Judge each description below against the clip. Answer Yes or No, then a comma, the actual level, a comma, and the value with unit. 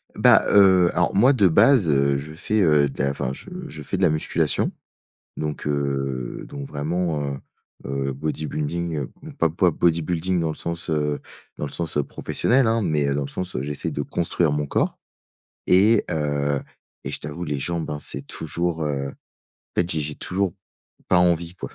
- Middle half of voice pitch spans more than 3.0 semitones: Yes, average, 3.4 semitones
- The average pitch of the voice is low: Yes, very low, 80 Hz